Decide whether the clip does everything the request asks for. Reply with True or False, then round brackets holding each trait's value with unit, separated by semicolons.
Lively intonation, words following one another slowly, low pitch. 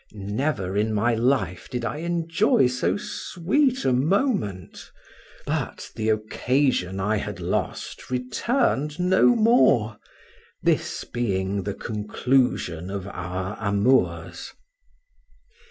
True (6.9 semitones; 105 wpm; 115 Hz)